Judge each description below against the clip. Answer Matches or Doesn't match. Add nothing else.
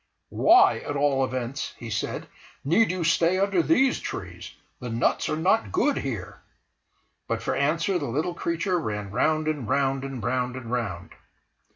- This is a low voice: Doesn't match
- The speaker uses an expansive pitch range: Matches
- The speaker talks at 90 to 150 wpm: Doesn't match